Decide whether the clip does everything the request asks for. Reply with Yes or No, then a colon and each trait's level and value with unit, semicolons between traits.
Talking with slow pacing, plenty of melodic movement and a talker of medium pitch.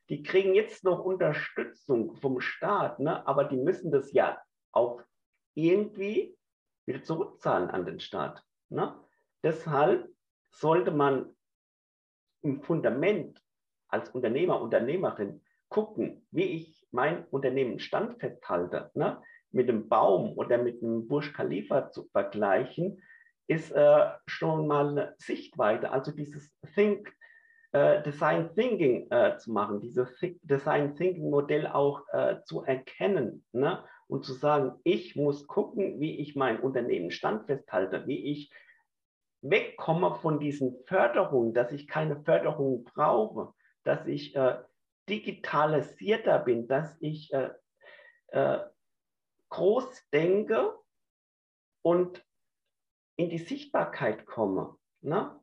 Yes: slow, 120 wpm; wide, 7.4 semitones; medium, 165 Hz